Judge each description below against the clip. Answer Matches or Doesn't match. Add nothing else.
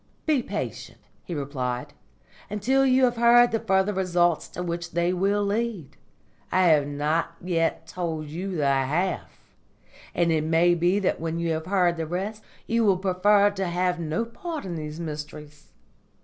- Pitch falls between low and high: Matches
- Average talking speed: Matches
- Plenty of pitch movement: Doesn't match